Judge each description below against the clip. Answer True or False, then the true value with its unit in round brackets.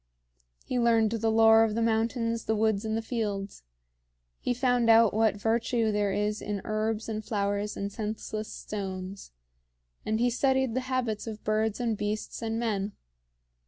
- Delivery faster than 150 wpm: True (160 wpm)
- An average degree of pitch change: False (1.6 semitones)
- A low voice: False (220 Hz)